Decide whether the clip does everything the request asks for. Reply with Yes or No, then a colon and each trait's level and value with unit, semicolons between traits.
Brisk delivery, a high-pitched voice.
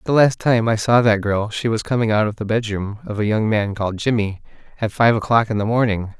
No: fast, 250 wpm; low, 110 Hz